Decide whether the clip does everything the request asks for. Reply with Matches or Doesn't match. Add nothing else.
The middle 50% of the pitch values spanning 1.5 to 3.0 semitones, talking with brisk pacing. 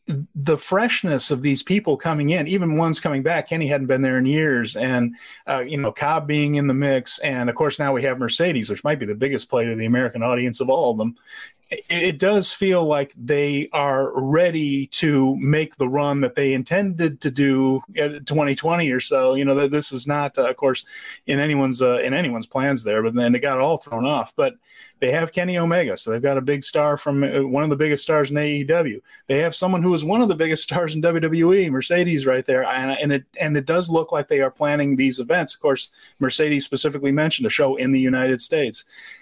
Doesn't match